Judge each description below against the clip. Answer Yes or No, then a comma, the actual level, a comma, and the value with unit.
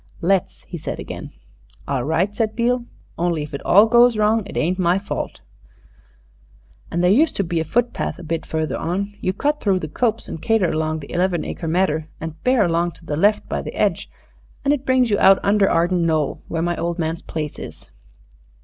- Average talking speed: No, fast, 210 wpm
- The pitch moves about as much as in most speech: Yes, average, 4.5 semitones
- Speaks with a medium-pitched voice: Yes, medium, 180 Hz